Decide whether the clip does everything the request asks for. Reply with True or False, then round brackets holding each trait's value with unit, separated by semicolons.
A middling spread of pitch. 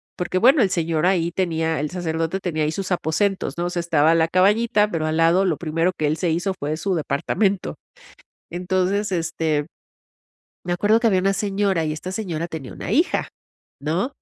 True (3.2 semitones)